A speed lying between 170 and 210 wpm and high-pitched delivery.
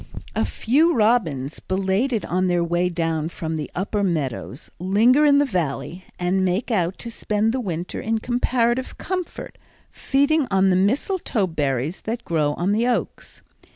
No: average, 155 wpm; high, 195 Hz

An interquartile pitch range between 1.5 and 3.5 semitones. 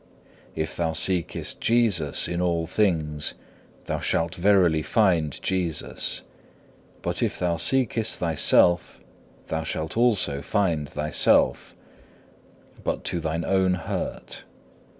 Yes: average, 3.2 semitones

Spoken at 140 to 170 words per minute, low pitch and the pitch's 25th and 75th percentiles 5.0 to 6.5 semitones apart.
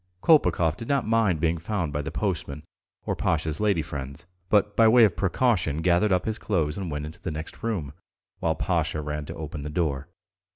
No: average, 200 wpm; very low, 85 Hz; wide, 5.5 semitones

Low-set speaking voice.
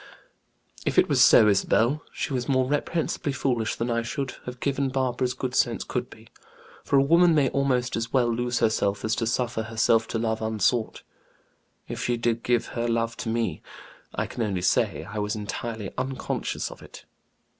Yes: low, 120 Hz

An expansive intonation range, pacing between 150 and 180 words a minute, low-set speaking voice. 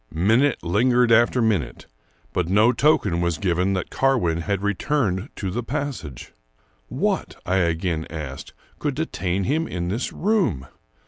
No: wide, 6.5 semitones; average, 140 wpm; low, 100 Hz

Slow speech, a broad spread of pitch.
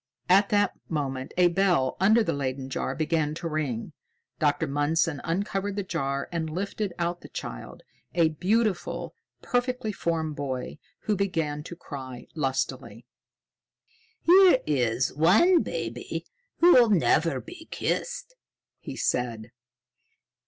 Yes: slow, 125 wpm; wide, 6.3 semitones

